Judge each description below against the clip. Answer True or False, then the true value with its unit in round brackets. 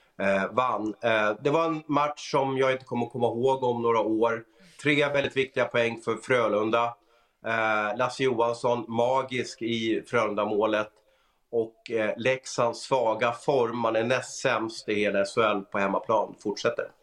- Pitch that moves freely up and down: False (3.0 semitones)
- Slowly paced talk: True (130 wpm)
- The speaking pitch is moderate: False (115 Hz)